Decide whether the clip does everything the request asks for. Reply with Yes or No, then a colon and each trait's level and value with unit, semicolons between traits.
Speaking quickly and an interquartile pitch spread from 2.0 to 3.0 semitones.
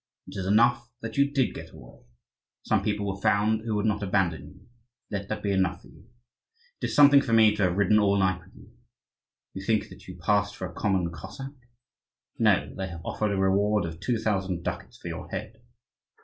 Yes: fast, 210 wpm; narrow, 2.5 semitones